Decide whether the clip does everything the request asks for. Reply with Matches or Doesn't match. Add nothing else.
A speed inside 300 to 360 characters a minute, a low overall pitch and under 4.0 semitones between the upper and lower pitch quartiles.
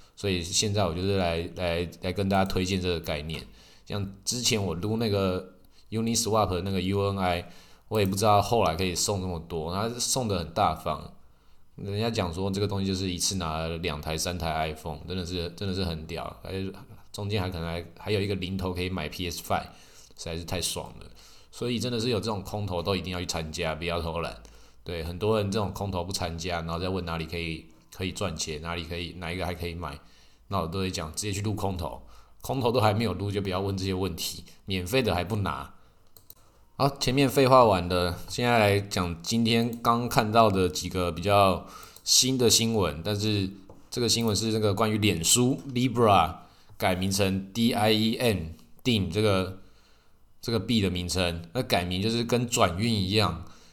Matches